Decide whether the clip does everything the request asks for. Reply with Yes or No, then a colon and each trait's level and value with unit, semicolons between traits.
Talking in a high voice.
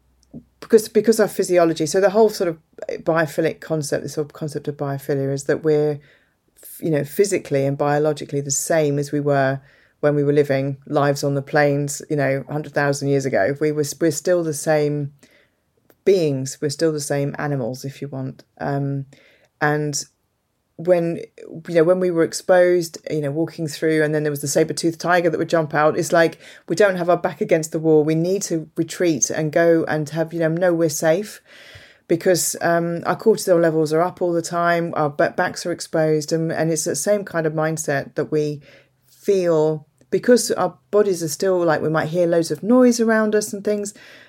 No: medium, 160 Hz